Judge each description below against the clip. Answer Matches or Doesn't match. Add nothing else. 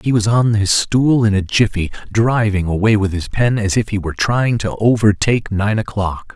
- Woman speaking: Doesn't match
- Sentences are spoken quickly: Matches